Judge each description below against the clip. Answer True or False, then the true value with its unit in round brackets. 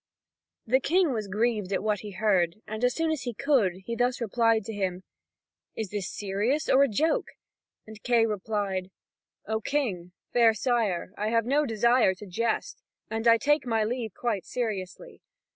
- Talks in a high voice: True (225 Hz)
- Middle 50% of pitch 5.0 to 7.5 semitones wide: False (3.4 semitones)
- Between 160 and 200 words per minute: True (175 wpm)